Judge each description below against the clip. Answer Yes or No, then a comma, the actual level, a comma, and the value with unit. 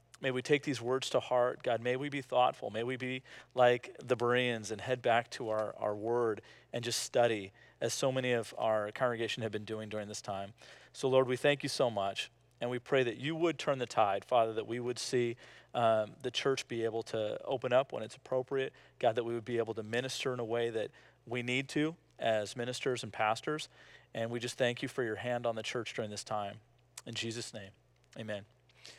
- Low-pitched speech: Yes, low, 120 Hz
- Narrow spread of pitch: Yes, narrow, 2.2 semitones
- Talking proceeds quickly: Yes, fast, 225 wpm